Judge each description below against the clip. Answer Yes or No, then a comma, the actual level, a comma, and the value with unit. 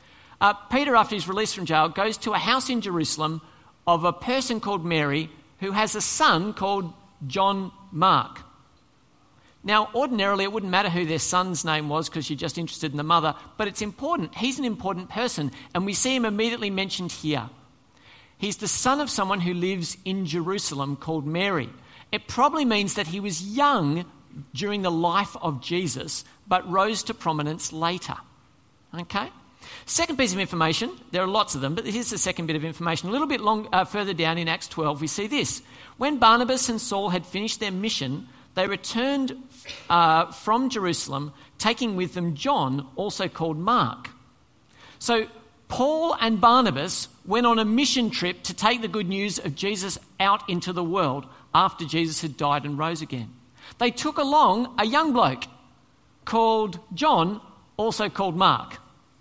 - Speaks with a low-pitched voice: No, high, 190 Hz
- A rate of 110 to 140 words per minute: No, average, 175 wpm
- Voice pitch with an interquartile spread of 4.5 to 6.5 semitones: Yes, average, 5.2 semitones